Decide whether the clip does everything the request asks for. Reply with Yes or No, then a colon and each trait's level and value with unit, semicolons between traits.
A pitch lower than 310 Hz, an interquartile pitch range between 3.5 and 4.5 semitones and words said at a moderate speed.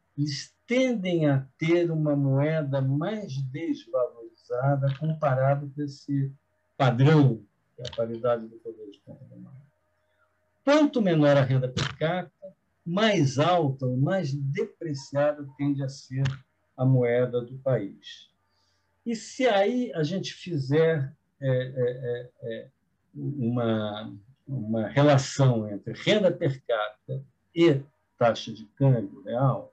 No: medium, 140 Hz; average, 4.2 semitones; slow, 115 wpm